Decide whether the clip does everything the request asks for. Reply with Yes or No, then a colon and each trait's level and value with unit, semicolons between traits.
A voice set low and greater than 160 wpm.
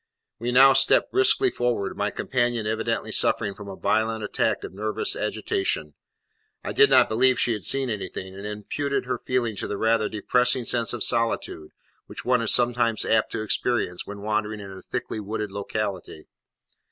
Yes: low, 110 Hz; average, 175 wpm